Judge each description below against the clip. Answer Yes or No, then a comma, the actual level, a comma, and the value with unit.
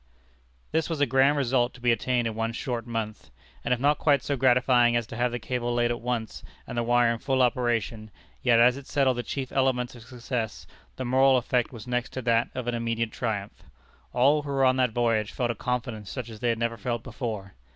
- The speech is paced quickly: Yes, fast, 230 wpm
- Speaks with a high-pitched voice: No, low, 120 Hz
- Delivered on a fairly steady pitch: Yes, narrow, 1.9 semitones